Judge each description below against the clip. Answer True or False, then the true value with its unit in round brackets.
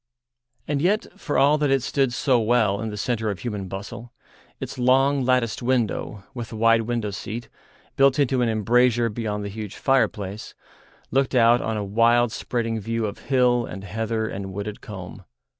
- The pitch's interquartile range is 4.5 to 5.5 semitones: False (3.1 semitones)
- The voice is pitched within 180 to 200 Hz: False (115 Hz)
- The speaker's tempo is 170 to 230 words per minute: True (175 wpm)